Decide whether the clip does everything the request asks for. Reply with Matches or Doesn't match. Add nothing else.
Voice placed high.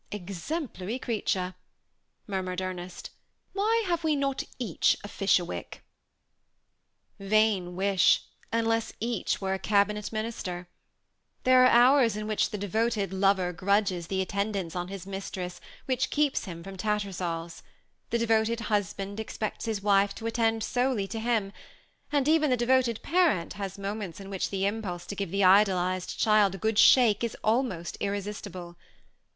Matches